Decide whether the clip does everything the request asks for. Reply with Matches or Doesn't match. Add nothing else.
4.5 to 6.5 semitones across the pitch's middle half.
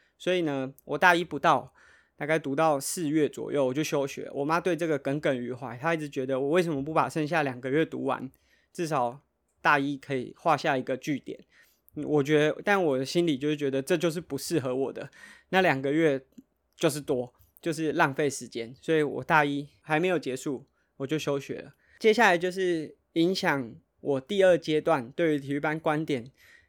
Doesn't match